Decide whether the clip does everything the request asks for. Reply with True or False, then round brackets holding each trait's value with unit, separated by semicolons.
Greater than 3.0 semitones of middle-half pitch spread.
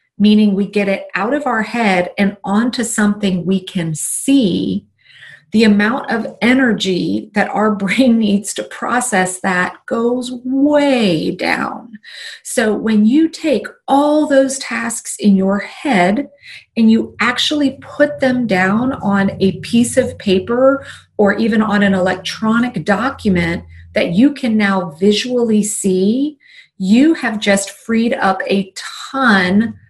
True (4.7 semitones)